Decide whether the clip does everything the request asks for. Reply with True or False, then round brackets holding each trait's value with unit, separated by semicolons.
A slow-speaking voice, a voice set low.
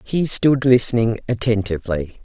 True (105 wpm; 115 Hz)